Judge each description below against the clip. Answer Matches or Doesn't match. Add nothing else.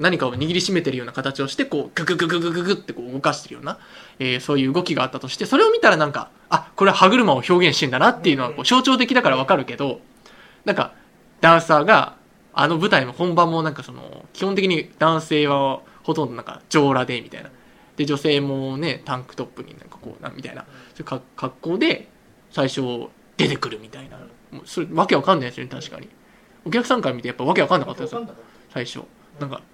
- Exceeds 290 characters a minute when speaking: Matches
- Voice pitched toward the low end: Doesn't match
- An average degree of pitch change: Matches